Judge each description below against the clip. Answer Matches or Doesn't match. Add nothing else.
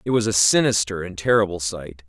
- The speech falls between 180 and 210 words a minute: Matches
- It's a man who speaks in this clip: Matches